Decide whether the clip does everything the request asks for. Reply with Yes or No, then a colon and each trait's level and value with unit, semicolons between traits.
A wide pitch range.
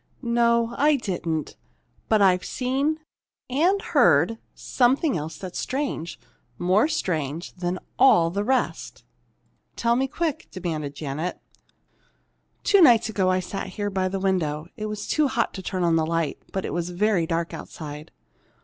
Yes: wide, 6.4 semitones